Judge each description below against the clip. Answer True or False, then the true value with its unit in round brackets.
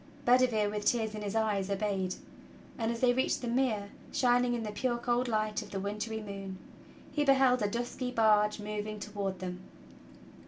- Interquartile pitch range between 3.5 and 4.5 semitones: False (2.9 semitones)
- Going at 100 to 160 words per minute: False (180 wpm)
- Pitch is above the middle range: True (215 Hz)